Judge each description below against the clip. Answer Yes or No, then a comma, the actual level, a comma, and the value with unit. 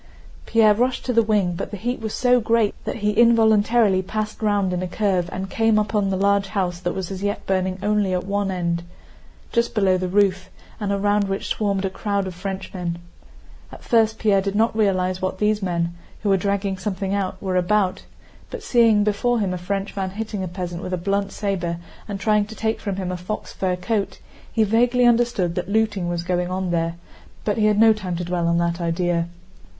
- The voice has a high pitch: Yes, high, 200 Hz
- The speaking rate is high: Yes, fast, 210 wpm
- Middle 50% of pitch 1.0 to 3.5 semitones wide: Yes, average, 2.7 semitones